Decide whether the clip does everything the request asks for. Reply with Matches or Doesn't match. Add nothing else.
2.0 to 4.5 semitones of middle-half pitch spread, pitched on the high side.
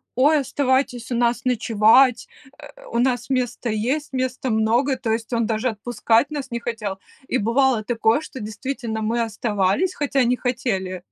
Matches